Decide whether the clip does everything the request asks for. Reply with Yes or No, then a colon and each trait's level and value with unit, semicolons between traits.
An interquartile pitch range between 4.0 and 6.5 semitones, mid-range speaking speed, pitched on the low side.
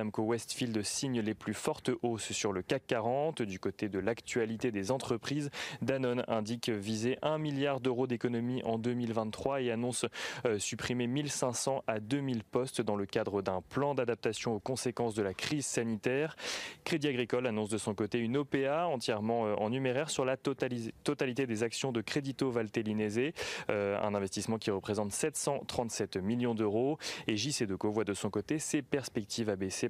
No: average, 3.5 semitones; average, 170 wpm; low, 120 Hz